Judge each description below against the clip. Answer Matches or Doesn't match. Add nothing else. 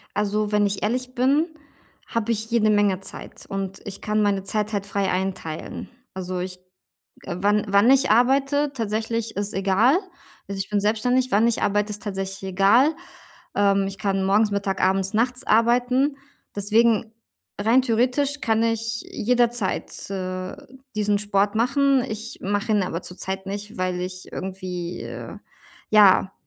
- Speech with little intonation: Doesn't match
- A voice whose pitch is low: Doesn't match